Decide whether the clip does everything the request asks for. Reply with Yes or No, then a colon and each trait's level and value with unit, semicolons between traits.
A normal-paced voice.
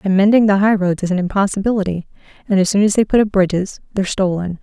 No: fast, 220 wpm